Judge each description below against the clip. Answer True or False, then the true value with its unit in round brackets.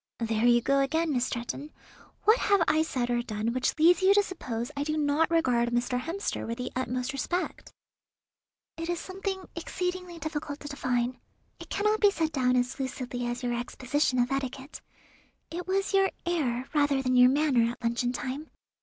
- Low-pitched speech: False (275 Hz)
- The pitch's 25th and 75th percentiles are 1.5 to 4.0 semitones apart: False (5.2 semitones)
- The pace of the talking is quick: False (180 wpm)